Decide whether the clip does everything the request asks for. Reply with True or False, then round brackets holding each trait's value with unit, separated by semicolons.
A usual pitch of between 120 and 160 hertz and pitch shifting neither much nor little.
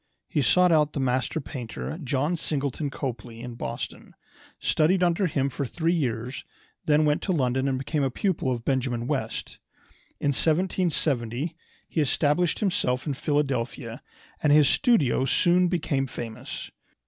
True (140 Hz; 4.2 semitones)